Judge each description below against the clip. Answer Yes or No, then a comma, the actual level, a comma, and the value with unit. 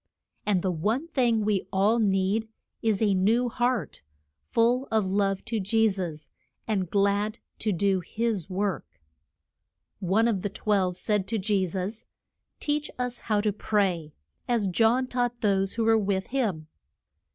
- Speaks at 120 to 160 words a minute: Yes, average, 150 wpm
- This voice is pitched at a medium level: No, high, 205 Hz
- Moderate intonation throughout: Yes, average, 3.1 semitones